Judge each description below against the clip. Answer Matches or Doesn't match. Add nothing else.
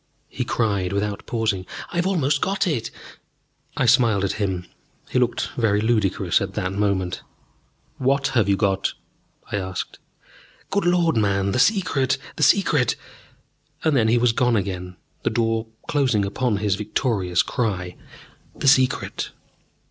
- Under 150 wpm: Matches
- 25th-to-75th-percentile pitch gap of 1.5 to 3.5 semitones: Doesn't match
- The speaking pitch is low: Matches